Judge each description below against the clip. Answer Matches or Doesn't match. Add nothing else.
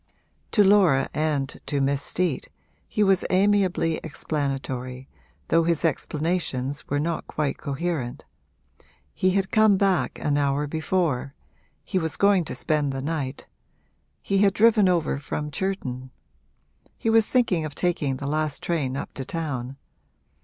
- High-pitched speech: Doesn't match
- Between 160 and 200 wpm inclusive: Doesn't match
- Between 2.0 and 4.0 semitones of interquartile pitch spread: Doesn't match